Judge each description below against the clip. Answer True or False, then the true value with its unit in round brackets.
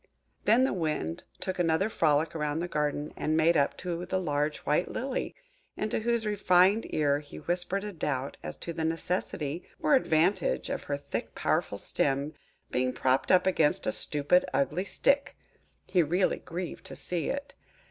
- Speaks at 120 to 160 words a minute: False (170 wpm)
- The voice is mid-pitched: True (165 Hz)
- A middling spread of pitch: True (4.1 semitones)